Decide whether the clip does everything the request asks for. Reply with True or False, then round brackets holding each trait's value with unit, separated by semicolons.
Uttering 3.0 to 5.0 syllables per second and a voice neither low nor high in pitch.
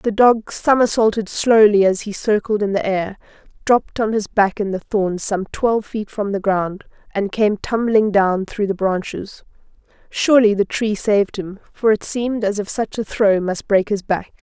False (4.7 syllables/s; 205 Hz)